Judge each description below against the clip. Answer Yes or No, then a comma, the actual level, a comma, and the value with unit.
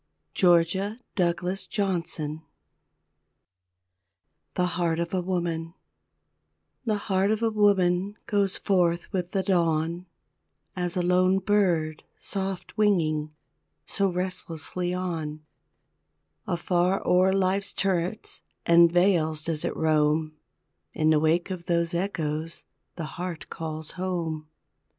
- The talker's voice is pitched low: No, medium, 175 Hz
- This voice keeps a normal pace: No, slow, 110 wpm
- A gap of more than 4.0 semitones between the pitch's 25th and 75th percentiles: No, narrow, 2.6 semitones